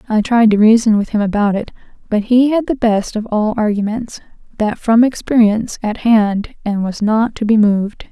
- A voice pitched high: Yes, high, 220 Hz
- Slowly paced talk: No, average, 200 wpm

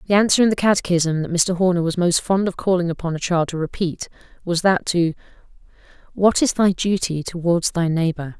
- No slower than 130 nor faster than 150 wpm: No, average, 200 wpm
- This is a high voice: No, medium, 175 Hz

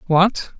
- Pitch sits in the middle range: Yes, medium, 180 Hz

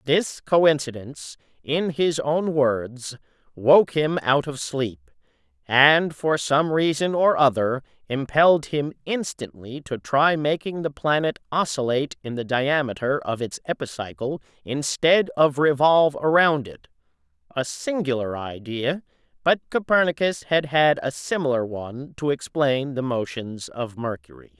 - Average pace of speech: No, slow, 125 wpm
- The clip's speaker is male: Yes, male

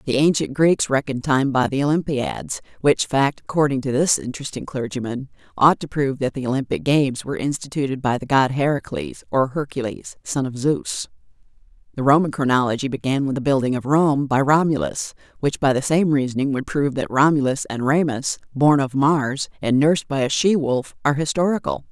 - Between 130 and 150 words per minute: No, average, 180 wpm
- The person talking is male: No, female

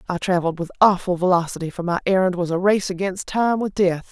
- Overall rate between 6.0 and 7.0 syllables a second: Yes, 6.1 syllables/s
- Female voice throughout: Yes, female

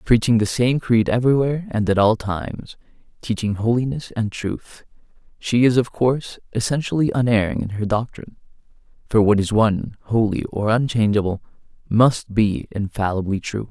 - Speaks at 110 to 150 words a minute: Yes, average, 145 wpm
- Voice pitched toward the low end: Yes, low, 115 Hz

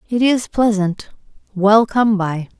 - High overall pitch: Yes, high, 210 Hz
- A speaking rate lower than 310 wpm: Yes, average, 140 wpm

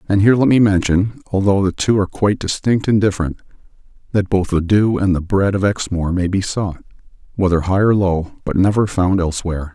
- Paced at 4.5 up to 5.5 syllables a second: No, 5.8 syllables/s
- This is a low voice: Yes, very low, 95 Hz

